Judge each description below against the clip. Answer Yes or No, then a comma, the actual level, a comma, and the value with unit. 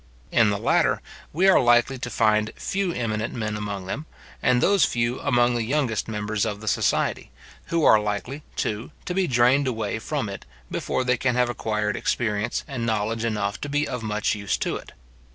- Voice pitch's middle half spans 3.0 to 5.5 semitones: Yes, average, 3.3 semitones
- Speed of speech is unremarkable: Yes, average, 190 wpm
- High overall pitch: No, low, 115 Hz